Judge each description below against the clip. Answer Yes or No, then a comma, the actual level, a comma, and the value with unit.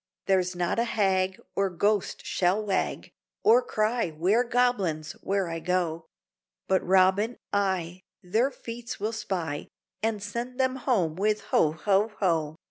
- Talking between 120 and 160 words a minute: Yes, average, 140 wpm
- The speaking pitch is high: Yes, high, 195 Hz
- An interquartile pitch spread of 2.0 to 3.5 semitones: No, average, 4.0 semitones